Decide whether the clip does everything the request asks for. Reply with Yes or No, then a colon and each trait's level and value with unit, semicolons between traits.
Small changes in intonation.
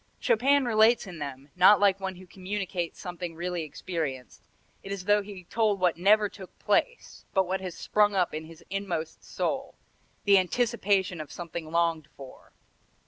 No: average, 3.3 semitones